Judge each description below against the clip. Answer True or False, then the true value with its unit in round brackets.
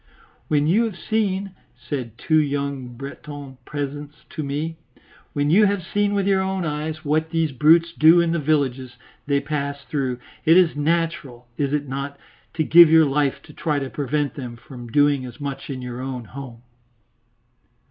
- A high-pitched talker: False (145 Hz)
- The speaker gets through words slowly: False (175 wpm)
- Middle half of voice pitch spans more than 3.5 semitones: False (3.0 semitones)